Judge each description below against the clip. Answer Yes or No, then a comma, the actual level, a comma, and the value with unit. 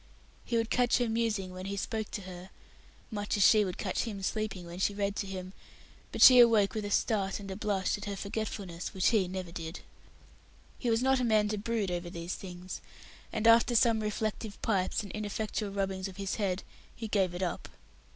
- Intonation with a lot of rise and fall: No, average, 2.8 semitones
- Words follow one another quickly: Yes, fast, 210 wpm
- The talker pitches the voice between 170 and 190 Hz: No, high, 200 Hz